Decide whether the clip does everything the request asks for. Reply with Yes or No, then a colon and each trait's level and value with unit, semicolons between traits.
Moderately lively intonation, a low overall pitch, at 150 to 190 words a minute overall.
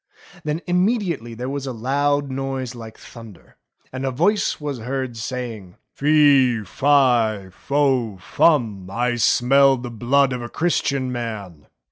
No: average, 3.4 semitones; low, 130 Hz; slow, 135 wpm